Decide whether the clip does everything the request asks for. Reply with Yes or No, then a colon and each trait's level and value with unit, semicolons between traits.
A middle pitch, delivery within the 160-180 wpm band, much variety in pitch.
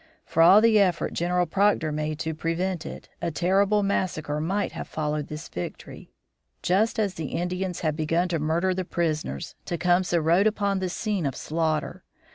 No: medium, 175 Hz; average, 170 wpm; average, 3.3 semitones